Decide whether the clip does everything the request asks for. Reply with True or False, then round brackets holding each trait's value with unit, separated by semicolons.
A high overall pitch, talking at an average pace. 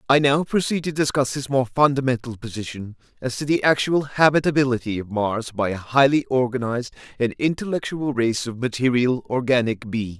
False (130 Hz; 160 wpm)